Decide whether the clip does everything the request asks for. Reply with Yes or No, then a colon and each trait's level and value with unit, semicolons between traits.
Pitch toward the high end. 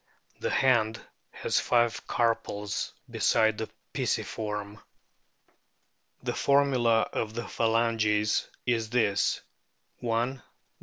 No: low, 115 Hz